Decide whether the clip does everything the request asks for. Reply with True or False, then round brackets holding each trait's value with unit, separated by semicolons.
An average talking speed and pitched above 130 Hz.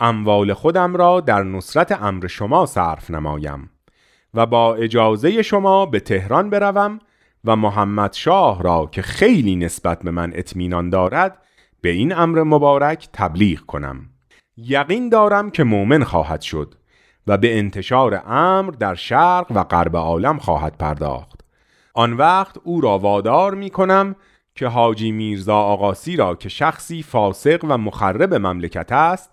False (140 wpm; 110 Hz)